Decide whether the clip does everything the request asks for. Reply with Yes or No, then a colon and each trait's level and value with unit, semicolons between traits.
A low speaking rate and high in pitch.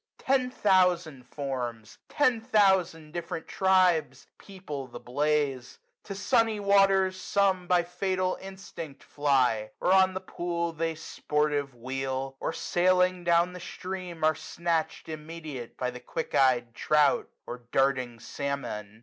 No: slow, 130 wpm; medium, 165 Hz